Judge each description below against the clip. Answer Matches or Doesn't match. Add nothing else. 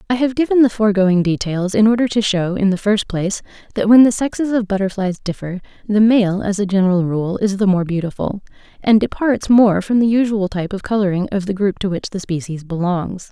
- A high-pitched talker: Matches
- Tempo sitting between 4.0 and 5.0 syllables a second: Doesn't match